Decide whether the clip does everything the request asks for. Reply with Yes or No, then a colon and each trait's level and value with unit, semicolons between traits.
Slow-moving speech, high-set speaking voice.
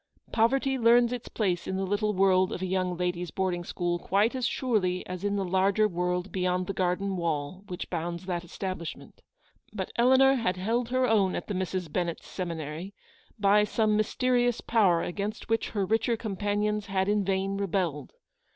No: average, 180 wpm; high, 195 Hz